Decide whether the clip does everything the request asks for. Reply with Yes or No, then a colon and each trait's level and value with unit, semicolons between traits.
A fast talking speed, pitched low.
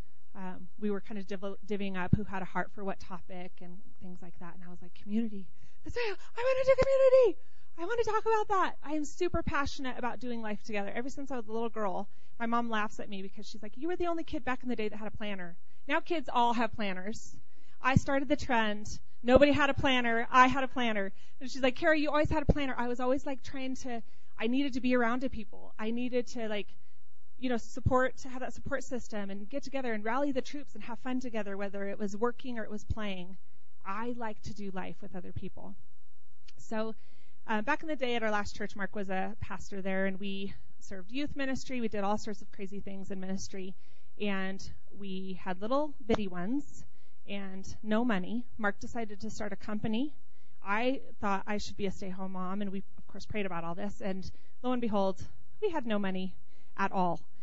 No: fast, 230 wpm; high, 215 Hz